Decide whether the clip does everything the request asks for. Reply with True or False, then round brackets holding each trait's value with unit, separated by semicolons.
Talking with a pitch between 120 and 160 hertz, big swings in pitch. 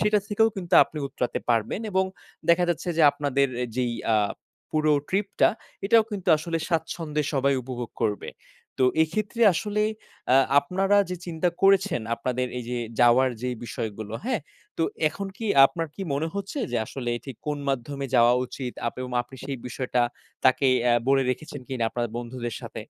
True (140 Hz; 6.5 semitones)